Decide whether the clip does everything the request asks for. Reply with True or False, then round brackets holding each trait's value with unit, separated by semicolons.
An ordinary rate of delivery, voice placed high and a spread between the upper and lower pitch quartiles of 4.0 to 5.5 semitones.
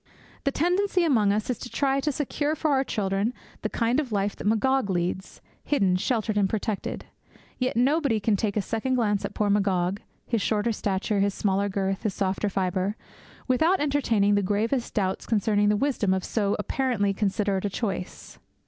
True (180 wpm; 210 Hz; 4.3 semitones)